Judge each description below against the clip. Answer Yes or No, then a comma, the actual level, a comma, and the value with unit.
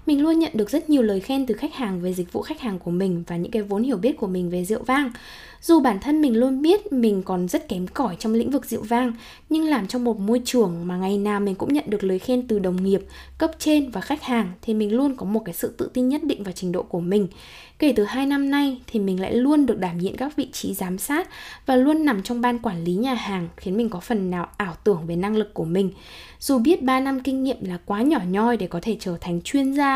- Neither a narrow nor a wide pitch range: No, wide, 6.1 semitones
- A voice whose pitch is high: Yes, high, 230 Hz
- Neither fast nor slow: No, fast, 280 wpm